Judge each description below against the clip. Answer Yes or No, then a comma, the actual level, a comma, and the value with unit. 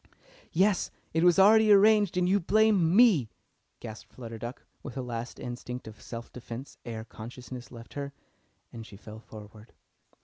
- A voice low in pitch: Yes, low, 125 Hz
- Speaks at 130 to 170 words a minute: Yes, average, 160 wpm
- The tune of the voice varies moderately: No, wide, 8.4 semitones